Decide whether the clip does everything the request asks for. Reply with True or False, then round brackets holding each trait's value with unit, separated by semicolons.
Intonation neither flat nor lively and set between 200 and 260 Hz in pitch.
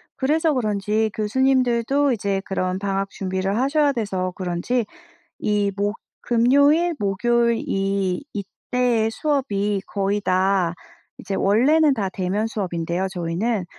True (4.3 semitones; 210 Hz)